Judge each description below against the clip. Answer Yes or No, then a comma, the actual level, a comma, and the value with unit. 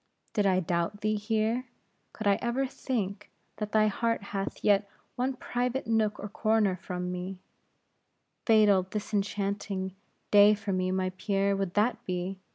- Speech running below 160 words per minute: Yes, average, 150 wpm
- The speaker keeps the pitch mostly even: Yes, narrow, 2.3 semitones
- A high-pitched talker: Yes, high, 205 Hz